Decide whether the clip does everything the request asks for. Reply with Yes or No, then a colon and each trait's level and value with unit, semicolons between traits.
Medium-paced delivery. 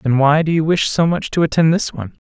No: fast, 290 wpm